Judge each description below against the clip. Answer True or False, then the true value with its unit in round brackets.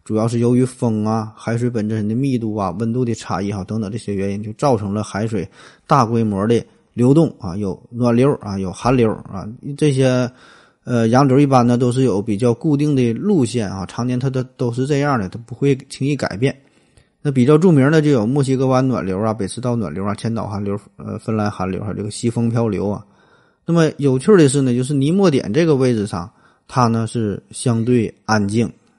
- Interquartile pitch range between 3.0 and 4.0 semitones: True (3.6 semitones)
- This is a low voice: True (120 Hz)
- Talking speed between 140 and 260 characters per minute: False (305 characters per minute)